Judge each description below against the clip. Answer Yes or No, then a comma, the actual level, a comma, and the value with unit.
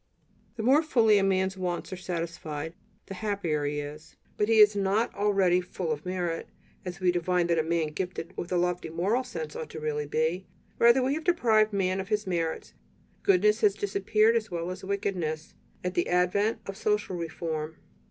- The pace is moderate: Yes, average, 190 wpm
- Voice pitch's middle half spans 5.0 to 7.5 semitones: No, average, 3.8 semitones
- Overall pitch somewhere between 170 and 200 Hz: Yes, medium, 185 Hz